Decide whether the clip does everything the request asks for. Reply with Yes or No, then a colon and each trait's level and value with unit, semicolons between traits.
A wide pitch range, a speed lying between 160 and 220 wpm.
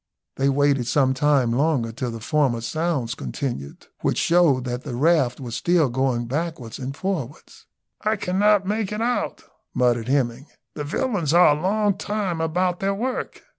Yes: wide, 6.2 semitones; average, 165 wpm